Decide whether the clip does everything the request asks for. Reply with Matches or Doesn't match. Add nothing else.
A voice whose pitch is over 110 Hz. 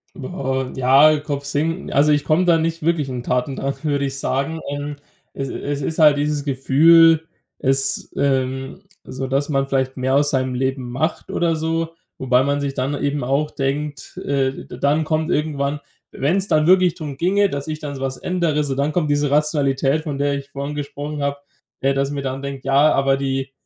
Matches